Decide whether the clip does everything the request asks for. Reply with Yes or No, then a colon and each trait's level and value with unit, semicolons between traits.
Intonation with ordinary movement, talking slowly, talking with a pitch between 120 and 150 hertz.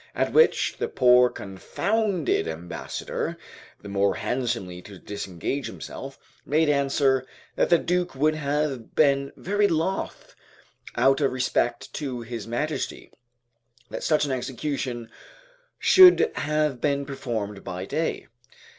Yes: average, 4.5 semitones; slow, 120 wpm; low, 135 Hz